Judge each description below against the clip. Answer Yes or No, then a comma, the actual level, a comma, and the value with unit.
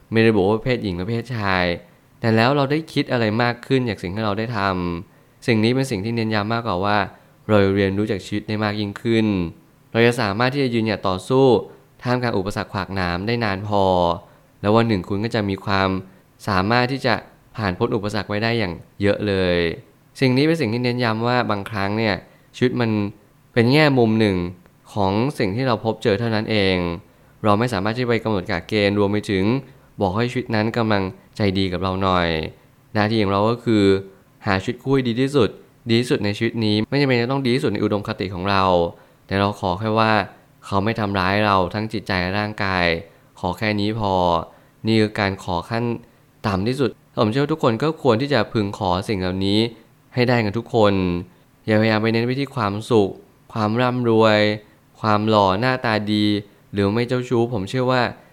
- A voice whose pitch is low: Yes, low, 110 Hz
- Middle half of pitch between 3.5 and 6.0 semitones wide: Yes, average, 3.8 semitones